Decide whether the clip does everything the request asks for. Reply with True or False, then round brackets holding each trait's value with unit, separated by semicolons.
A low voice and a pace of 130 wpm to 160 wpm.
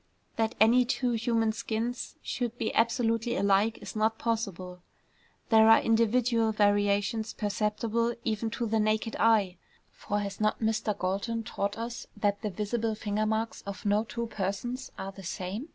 False (220 Hz; 155 wpm)